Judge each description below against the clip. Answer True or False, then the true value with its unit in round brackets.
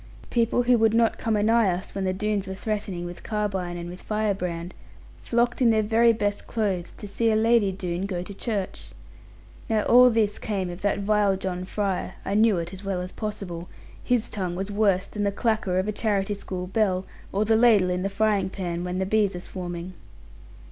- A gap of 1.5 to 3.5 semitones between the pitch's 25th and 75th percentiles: True (2.9 semitones)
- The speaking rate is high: True (210 wpm)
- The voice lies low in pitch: False (200 Hz)